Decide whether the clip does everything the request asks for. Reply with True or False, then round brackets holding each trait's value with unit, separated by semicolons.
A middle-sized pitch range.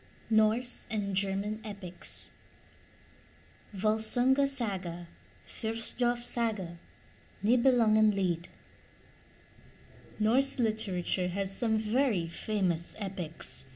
True (3.5 semitones)